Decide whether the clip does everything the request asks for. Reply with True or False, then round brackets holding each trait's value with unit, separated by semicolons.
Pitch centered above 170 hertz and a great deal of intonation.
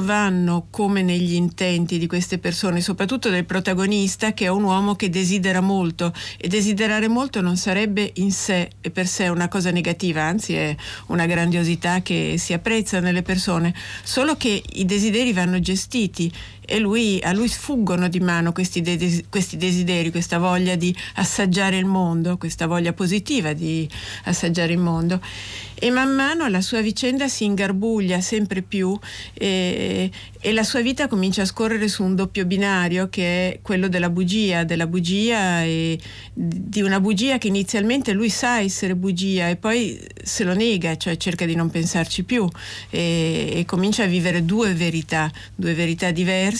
False (185 Hz; 2.9 semitones)